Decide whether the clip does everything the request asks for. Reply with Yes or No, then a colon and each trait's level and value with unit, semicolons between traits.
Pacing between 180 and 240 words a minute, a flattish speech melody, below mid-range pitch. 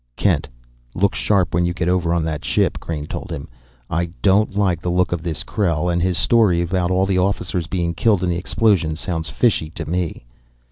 Yes: fast, 205 wpm; narrow, 2.0 semitones; very low, 90 Hz